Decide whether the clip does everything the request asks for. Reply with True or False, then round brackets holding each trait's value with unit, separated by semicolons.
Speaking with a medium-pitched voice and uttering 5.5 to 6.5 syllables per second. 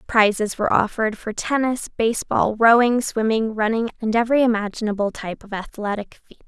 False (220 Hz; 5.8 syllables/s)